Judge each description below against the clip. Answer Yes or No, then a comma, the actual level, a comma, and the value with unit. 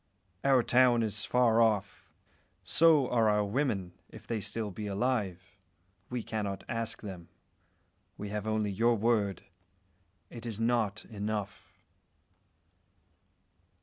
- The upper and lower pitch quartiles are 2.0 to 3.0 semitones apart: Yes, narrow, 2.6 semitones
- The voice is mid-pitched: No, low, 110 Hz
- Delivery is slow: Yes, slow, 115 wpm